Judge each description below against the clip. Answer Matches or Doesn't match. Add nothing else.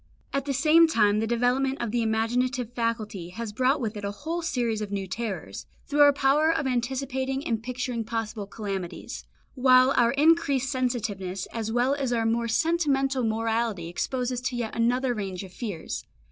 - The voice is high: Matches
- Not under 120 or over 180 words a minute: Matches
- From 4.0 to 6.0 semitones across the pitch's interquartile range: Doesn't match